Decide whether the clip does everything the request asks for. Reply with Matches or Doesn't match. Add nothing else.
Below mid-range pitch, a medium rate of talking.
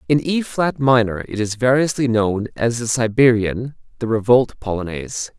Matches